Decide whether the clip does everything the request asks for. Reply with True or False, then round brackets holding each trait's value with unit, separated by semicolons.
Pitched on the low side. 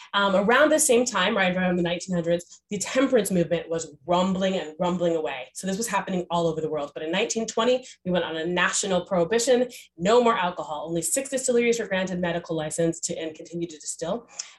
False (180 Hz)